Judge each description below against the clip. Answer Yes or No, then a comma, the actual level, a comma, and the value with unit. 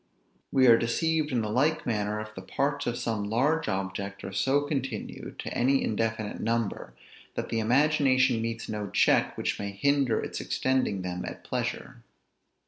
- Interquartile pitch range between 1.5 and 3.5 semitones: No, average, 4.4 semitones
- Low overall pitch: Yes, low, 115 Hz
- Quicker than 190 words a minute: No, average, 165 wpm